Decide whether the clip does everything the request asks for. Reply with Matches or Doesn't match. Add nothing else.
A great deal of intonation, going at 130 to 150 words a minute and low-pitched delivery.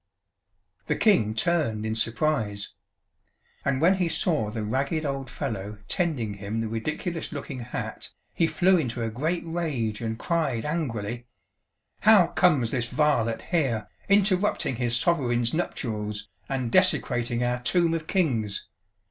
Matches